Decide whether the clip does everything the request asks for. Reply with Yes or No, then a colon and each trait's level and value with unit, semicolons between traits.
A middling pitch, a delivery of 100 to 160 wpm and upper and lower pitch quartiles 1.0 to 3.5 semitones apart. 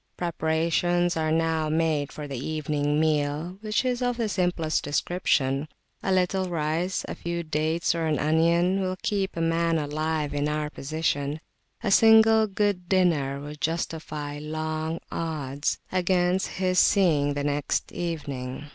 Yes: medium, 160 Hz; average, 145 wpm; average, 3.1 semitones